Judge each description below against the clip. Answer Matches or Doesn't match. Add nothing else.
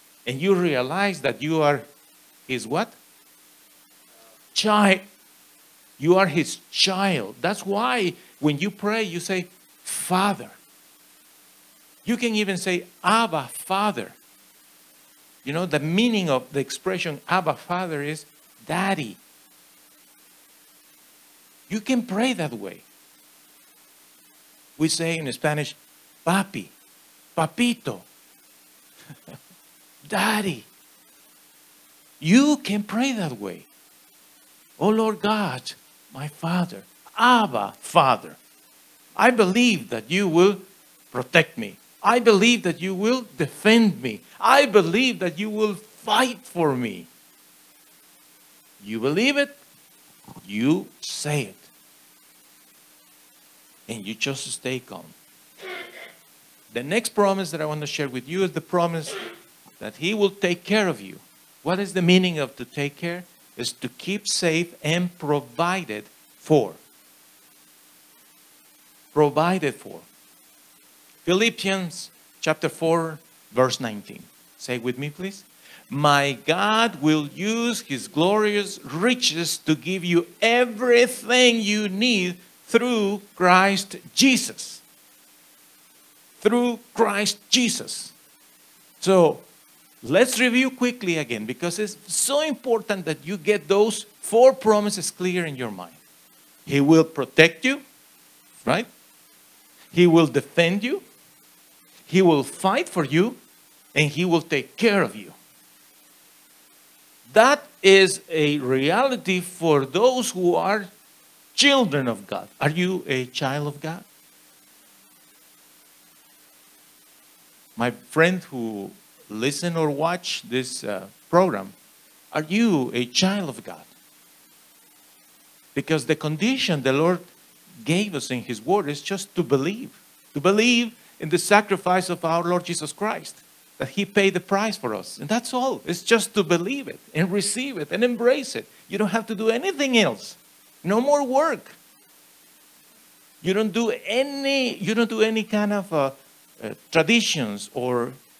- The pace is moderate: Doesn't match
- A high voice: Doesn't match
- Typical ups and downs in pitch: Doesn't match